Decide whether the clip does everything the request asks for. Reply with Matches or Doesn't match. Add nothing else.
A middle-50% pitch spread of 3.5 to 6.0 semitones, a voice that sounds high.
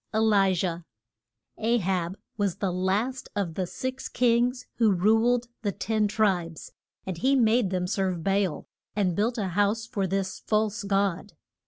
Doesn't match